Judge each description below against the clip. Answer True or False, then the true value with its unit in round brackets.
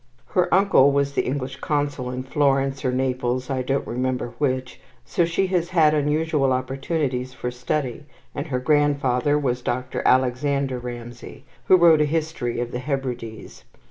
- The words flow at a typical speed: True (155 wpm)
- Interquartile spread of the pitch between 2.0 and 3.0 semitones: True (2.7 semitones)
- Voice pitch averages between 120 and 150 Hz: True (135 Hz)